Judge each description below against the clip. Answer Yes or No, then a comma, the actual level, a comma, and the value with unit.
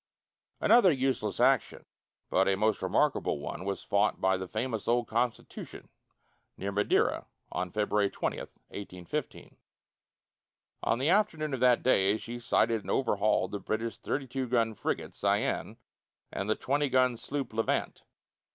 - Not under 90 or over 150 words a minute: Yes, average, 140 wpm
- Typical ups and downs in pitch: Yes, average, 4.2 semitones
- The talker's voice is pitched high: No, low, 115 Hz